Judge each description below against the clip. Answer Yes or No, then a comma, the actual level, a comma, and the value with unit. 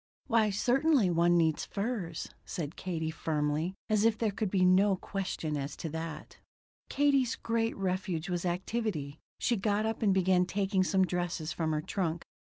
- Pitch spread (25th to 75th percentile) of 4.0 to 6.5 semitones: Yes, average, 4.4 semitones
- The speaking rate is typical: Yes, average, 165 wpm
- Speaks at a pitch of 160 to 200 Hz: Yes, medium, 185 Hz